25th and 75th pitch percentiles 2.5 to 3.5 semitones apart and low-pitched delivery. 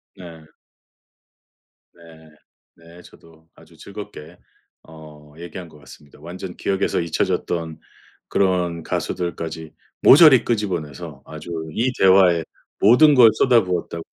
Yes: average, 2.9 semitones; very low, 85 Hz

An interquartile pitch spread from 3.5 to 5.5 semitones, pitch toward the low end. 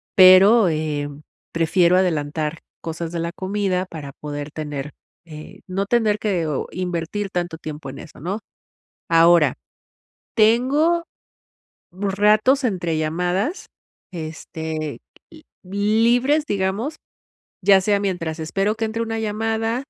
No: average, 5.0 semitones; medium, 185 Hz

